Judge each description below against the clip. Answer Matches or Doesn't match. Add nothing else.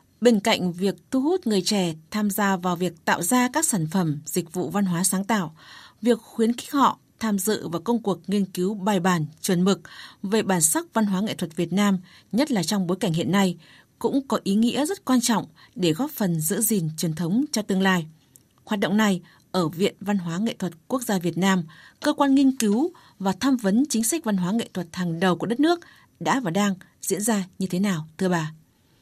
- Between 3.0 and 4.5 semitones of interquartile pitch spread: Matches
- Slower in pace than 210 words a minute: Doesn't match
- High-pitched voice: Matches